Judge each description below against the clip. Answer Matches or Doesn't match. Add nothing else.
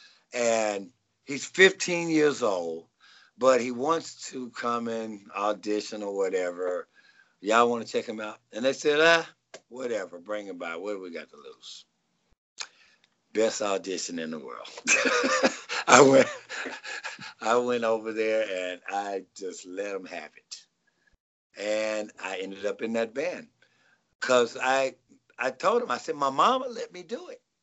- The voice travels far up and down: Matches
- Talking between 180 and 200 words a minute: Doesn't match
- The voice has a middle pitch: Doesn't match